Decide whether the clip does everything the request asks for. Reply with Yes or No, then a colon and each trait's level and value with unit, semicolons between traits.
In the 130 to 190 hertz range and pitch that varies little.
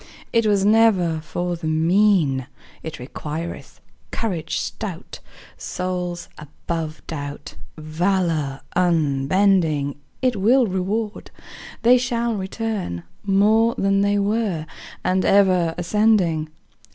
No: medium, 185 Hz; average, 4.7 semitones